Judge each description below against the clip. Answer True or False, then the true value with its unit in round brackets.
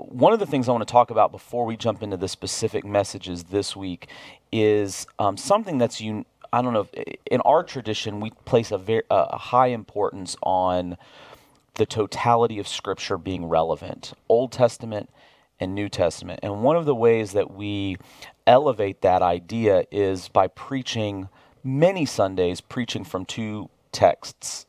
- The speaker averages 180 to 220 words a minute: False (165 wpm)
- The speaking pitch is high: False (105 Hz)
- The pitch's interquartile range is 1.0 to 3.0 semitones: False (3.6 semitones)